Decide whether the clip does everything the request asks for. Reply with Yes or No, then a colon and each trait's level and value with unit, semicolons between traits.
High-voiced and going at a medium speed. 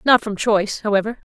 Yes: high, 215 Hz; average, 180 wpm